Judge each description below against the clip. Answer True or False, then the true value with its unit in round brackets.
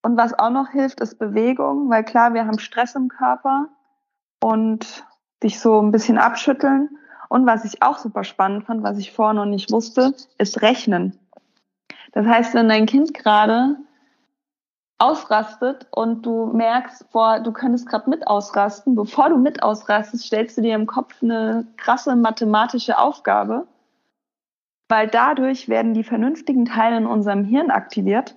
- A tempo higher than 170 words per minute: False (155 wpm)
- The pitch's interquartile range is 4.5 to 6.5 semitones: False (3.4 semitones)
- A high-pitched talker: True (230 Hz)